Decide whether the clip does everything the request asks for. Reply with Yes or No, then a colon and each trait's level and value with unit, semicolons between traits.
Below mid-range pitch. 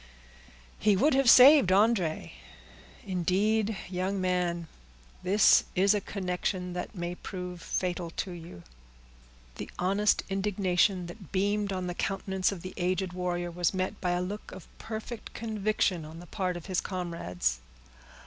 No: medium, 185 Hz